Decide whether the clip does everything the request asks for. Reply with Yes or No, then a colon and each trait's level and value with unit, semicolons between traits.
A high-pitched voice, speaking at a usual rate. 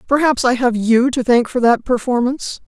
Yes: high, 245 Hz; average, 195 wpm